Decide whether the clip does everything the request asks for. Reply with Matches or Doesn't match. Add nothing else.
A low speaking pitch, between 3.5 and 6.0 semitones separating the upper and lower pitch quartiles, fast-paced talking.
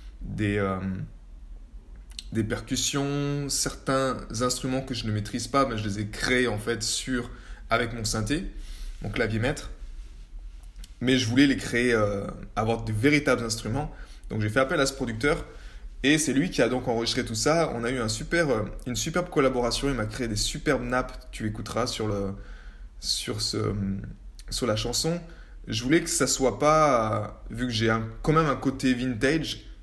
Doesn't match